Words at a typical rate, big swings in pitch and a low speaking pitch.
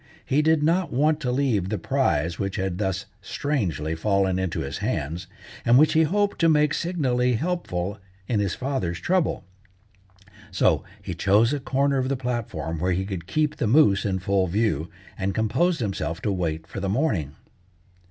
Yes: average, 175 wpm; wide, 7.6 semitones; low, 105 Hz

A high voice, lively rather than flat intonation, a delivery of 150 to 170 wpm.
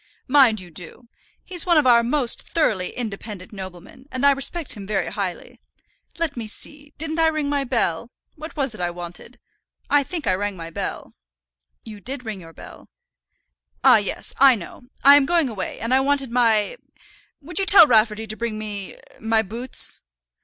No: high, 235 Hz; wide, 5.7 semitones; average, 180 wpm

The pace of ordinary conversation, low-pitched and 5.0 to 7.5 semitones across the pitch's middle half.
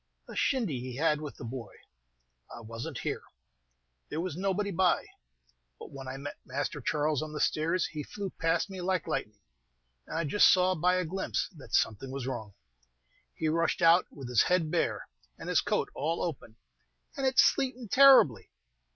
No: average, 180 wpm; medium, 155 Hz; wide, 5.5 semitones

